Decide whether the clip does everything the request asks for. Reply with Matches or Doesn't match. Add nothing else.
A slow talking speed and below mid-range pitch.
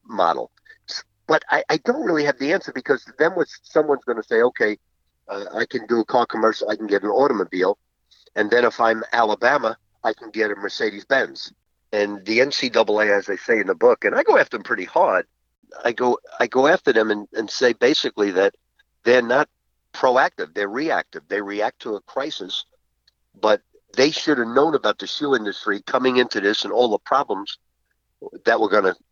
Doesn't match